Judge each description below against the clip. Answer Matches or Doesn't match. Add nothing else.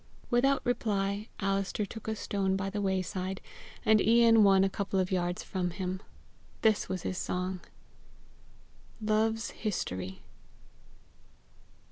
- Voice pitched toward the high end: Matches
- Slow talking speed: Matches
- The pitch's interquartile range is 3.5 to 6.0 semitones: Doesn't match